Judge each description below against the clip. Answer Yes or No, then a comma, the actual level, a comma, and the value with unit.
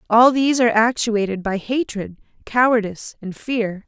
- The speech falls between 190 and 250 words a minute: No, average, 140 wpm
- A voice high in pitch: Yes, high, 225 Hz